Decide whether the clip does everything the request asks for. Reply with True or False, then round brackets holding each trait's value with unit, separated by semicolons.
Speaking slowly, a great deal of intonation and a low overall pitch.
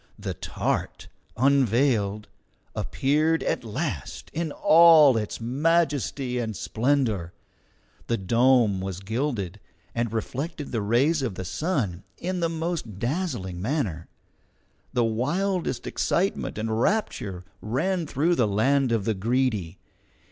True (120 wpm; 6.1 semitones; 125 Hz)